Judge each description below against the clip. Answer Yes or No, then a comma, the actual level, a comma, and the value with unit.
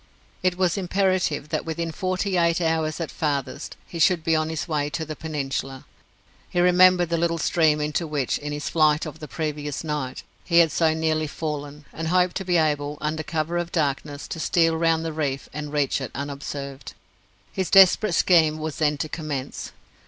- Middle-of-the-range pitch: Yes, medium, 155 Hz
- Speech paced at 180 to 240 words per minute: Yes, average, 190 wpm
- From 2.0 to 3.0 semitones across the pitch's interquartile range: Yes, narrow, 2.4 semitones